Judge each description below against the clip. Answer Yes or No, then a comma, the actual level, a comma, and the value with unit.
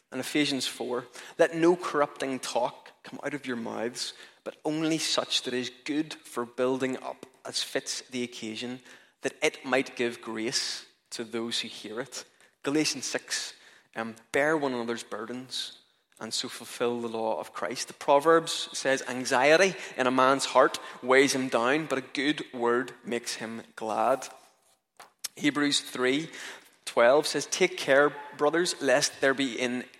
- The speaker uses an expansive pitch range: No, average, 3.2 semitones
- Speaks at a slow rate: No, average, 155 wpm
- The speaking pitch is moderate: No, low, 130 Hz